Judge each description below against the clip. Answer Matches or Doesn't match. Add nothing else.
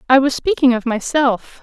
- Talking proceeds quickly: Doesn't match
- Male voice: Doesn't match